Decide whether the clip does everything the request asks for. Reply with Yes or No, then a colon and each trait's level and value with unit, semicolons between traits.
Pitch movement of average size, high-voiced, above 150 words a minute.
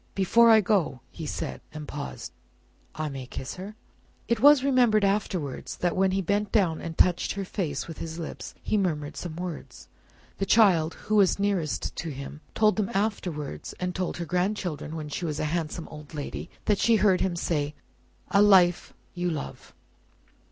No: average, 4.6 semitones; medium, 180 Hz; average, 180 wpm